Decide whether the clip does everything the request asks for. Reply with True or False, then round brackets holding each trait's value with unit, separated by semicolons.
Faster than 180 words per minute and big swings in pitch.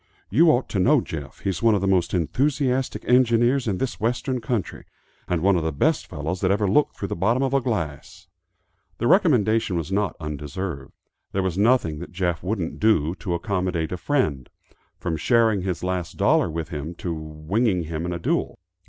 True (190 wpm; 6.0 semitones)